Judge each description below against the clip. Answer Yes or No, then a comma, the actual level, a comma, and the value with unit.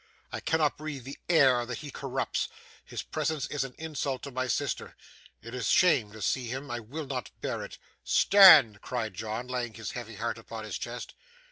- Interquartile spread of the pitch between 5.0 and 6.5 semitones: No, average, 3.9 semitones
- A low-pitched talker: Yes, low, 125 Hz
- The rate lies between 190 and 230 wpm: Yes, average, 195 wpm